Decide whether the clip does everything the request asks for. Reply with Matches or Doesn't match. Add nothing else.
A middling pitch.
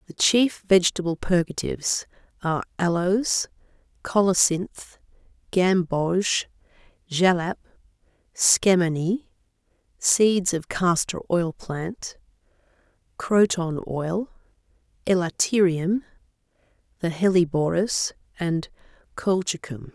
Matches